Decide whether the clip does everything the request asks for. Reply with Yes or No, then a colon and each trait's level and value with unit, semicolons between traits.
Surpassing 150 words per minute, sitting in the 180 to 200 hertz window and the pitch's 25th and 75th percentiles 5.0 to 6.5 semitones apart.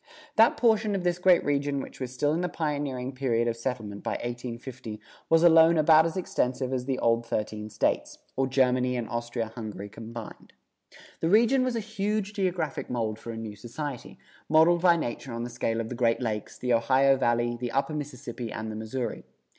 No: average, 195 wpm; low, 130 Hz; wide, 5.6 semitones